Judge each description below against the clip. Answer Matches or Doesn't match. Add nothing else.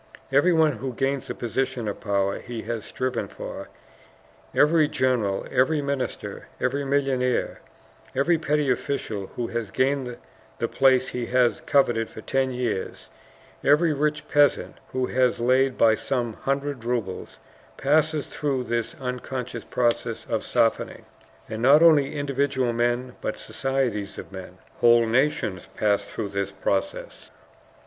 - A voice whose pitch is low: Matches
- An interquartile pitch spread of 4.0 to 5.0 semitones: Doesn't match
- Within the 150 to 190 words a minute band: Doesn't match